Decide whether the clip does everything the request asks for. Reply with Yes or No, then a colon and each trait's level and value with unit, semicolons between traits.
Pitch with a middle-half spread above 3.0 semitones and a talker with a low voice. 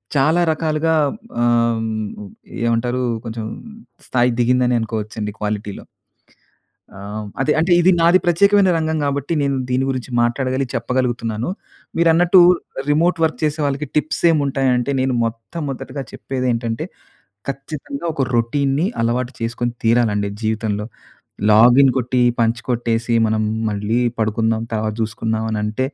Yes: average, 4.0 semitones; low, 125 Hz